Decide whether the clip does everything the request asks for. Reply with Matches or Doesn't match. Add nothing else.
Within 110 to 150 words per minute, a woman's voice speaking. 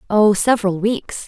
Matches